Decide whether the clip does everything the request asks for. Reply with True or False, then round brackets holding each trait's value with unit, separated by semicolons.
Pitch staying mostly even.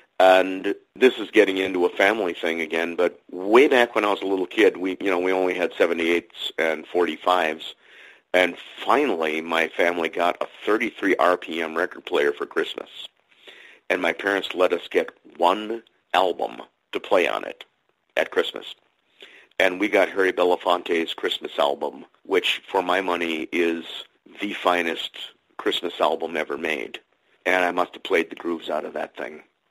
True (2.1 semitones)